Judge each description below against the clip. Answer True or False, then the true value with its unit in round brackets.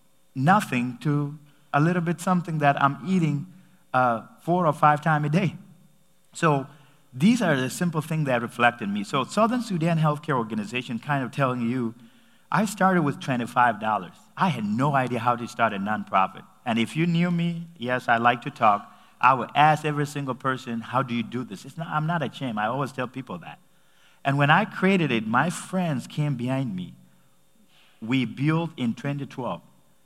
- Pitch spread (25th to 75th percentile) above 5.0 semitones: True (5.4 semitones)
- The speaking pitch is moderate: True (145 Hz)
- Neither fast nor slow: True (185 wpm)